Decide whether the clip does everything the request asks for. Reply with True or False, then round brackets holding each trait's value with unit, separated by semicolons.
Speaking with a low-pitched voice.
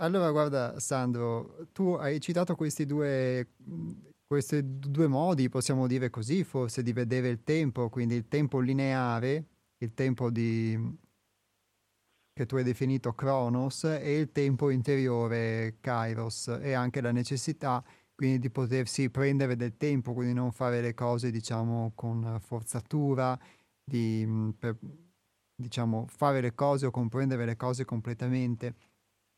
True (125 Hz)